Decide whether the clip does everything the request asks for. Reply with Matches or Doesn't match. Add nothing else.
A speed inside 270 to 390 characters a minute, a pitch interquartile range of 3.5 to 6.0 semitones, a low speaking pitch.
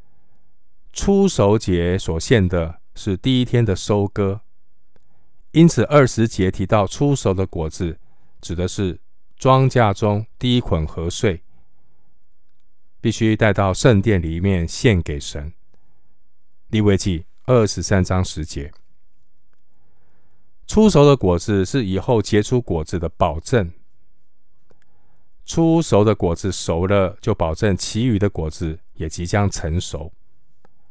Doesn't match